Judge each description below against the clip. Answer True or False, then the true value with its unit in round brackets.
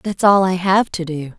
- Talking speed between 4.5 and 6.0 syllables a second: True (4.6 syllables/s)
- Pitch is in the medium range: True (180 Hz)